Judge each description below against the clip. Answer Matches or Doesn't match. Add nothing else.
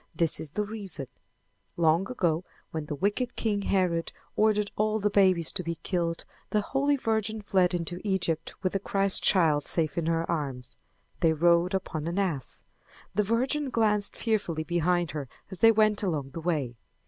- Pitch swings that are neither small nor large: Matches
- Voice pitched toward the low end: Doesn't match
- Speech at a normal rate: Matches